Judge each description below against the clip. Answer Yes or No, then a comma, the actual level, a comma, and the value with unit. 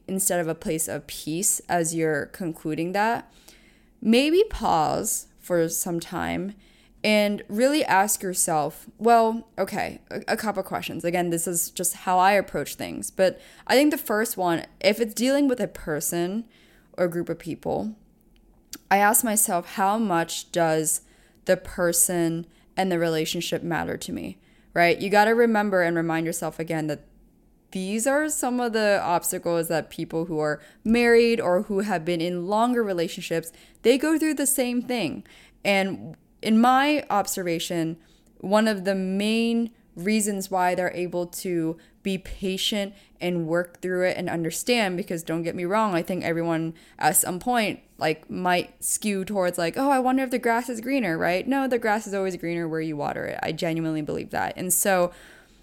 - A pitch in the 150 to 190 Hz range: Yes, medium, 185 Hz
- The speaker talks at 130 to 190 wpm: Yes, average, 170 wpm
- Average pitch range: Yes, average, 4.4 semitones